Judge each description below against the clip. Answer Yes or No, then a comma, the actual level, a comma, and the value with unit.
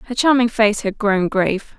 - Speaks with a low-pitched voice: No, high, 220 Hz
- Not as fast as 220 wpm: Yes, average, 200 wpm